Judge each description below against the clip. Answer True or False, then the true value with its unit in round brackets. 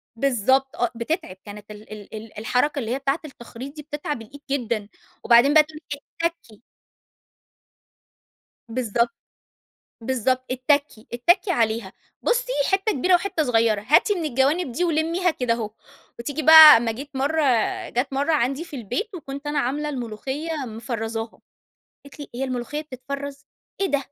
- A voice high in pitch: True (270 Hz)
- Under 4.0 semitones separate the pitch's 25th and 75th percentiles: False (4.6 semitones)